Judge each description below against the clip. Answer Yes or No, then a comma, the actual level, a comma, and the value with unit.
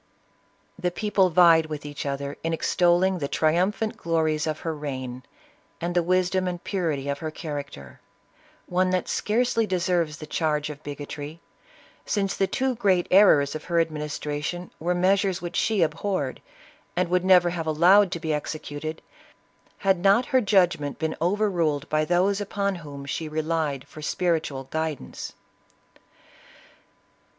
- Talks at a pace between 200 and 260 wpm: No, average, 155 wpm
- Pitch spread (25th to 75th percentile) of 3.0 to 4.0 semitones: Yes, average, 3.5 semitones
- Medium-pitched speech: Yes, medium, 165 Hz